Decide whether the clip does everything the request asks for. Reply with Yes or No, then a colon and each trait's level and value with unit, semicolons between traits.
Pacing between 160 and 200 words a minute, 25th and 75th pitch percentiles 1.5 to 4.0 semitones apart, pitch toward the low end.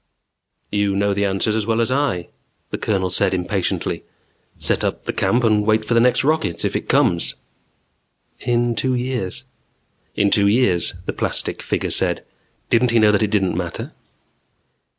Yes: average, 170 wpm; average, 3.6 semitones; low, 105 Hz